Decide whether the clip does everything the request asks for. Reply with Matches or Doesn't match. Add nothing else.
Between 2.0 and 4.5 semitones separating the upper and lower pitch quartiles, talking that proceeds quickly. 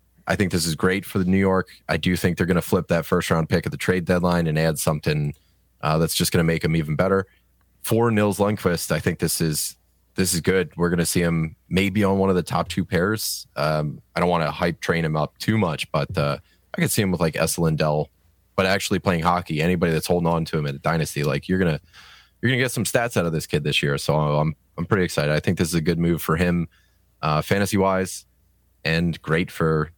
Matches